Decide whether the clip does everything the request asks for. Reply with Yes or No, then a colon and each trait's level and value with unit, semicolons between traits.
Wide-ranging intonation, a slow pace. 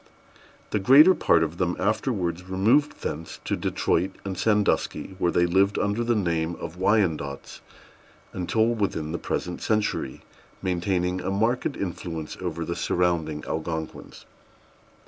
No: average, 3.7 semitones; slow, 130 wpm